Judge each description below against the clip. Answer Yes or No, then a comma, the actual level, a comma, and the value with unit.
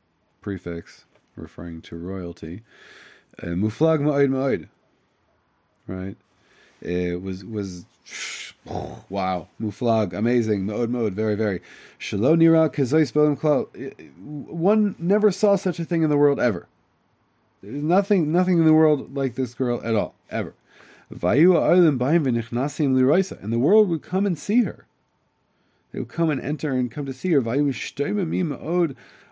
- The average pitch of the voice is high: No, low, 130 Hz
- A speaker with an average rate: No, slow, 125 wpm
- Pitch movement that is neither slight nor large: No, wide, 7.3 semitones